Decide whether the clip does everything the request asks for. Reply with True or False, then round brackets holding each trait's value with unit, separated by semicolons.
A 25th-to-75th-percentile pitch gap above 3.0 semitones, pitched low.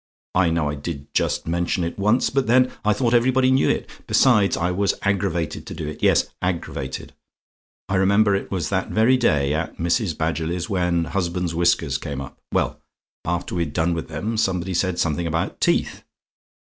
True (3.6 semitones; 90 Hz)